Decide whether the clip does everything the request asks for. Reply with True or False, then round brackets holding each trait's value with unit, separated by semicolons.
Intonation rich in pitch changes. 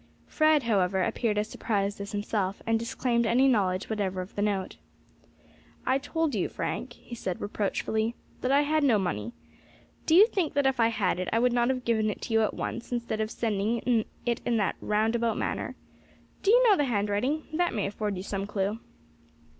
False (3.7 semitones)